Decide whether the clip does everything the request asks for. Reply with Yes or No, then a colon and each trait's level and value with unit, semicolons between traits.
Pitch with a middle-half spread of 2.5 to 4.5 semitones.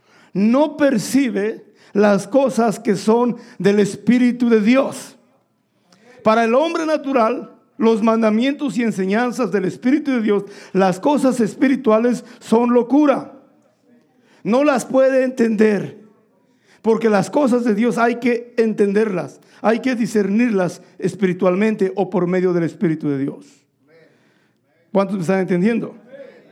Yes: average, 3.8 semitones